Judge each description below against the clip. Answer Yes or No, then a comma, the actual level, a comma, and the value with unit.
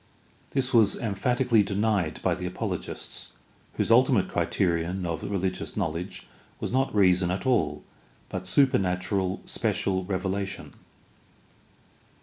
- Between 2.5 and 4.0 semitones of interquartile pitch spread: Yes, average, 3.3 semitones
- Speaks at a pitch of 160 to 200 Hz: No, very low, 95 Hz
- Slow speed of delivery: Yes, slow, 110 wpm